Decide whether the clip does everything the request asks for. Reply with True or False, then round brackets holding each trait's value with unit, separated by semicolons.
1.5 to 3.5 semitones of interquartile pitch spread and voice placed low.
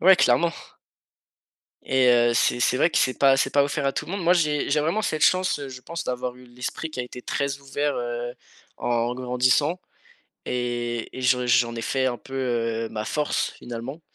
True (3.2 semitones; 130 Hz)